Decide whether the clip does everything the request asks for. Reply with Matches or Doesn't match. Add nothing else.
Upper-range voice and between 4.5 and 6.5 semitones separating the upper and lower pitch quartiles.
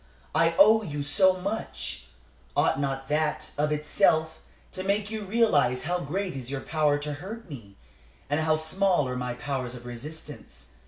Doesn't match